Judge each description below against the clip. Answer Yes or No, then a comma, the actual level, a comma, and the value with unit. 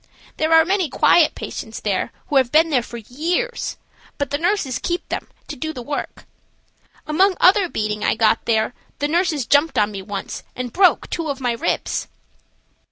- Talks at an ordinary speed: Yes, average, 180 wpm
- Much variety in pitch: Yes, wide, 6.5 semitones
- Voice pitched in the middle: No, very high, 290 Hz